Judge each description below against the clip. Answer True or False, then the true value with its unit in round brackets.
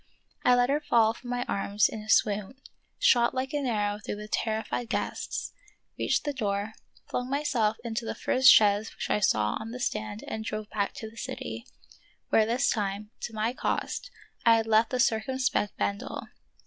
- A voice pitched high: True (225 Hz)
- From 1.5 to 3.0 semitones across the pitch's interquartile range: True (2.7 semitones)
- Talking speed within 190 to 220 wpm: True (200 wpm)